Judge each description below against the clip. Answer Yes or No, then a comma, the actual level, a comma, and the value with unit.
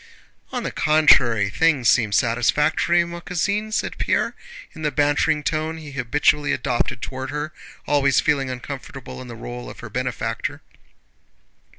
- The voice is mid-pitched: Yes, medium, 145 Hz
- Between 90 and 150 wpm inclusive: Yes, average, 145 wpm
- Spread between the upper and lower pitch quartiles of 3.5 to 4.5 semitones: Yes, average, 3.9 semitones